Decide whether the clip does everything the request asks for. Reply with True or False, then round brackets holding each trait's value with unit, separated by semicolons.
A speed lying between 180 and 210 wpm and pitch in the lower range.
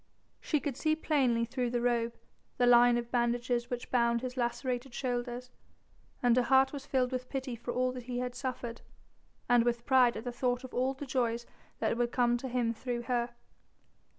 False (190 wpm; 245 Hz)